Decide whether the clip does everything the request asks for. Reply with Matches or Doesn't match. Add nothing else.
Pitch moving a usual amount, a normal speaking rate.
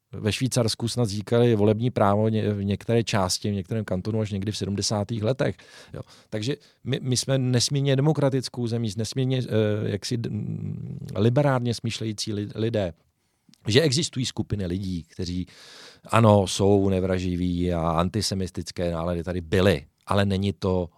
Matches